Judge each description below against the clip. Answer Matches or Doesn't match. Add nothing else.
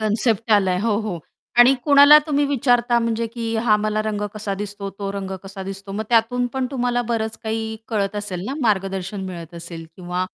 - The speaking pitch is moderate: Doesn't match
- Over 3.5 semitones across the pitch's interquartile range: Doesn't match